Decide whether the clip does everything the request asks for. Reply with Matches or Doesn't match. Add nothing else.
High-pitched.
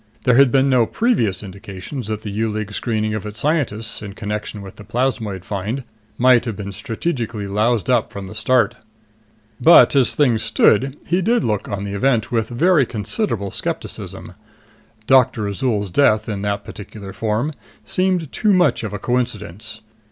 Doesn't match